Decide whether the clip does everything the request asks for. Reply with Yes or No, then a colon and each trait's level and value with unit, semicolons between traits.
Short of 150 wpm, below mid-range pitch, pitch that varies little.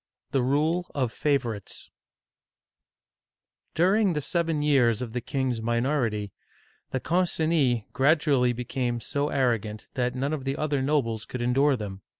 No: slow, 135 wpm; low, 130 Hz; average, 3.9 semitones